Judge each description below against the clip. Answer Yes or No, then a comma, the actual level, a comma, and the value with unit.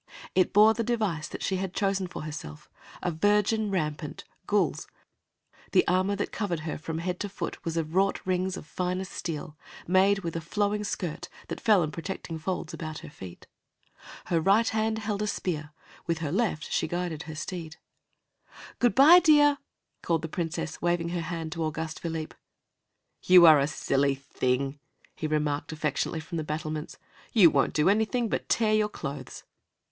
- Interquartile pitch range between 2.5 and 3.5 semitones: No, average, 4.5 semitones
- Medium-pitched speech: Yes, medium, 175 Hz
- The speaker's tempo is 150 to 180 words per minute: Yes, average, 175 wpm